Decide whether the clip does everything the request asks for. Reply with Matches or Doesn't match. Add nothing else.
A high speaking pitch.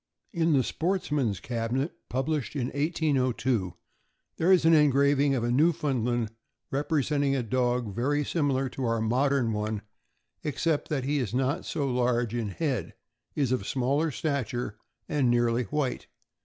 Doesn't match